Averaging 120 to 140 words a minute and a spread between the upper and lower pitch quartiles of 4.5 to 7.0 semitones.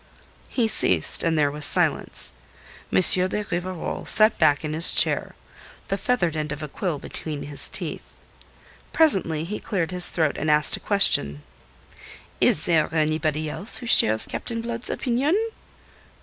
No: average, 150 wpm; average, 5.2 semitones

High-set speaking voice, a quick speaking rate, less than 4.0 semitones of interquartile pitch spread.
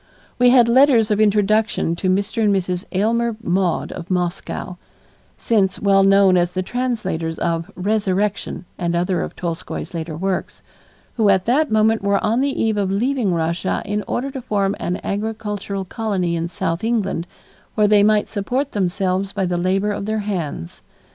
No: high, 200 Hz; average, 165 wpm; average, 3.1 semitones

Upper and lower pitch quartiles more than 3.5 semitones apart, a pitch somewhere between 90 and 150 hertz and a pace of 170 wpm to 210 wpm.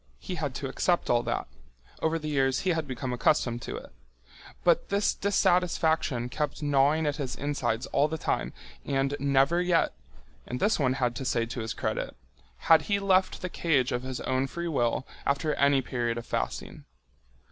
Yes: average, 4.5 semitones; medium, 140 Hz; average, 175 wpm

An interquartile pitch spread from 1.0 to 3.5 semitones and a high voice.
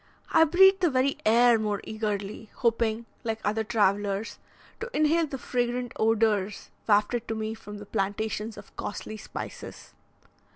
Yes: average, 2.8 semitones; high, 220 Hz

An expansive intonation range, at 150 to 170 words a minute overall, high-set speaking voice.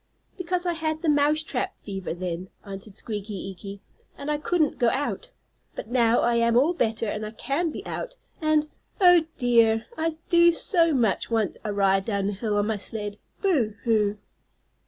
No: wide, 7.1 semitones; average, 180 wpm; high, 235 Hz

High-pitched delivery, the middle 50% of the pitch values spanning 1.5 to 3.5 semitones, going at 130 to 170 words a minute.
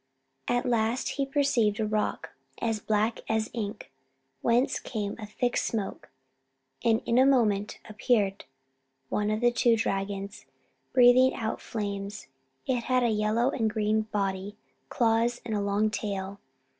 Yes: high, 220 Hz; narrow, 2.6 semitones; average, 145 wpm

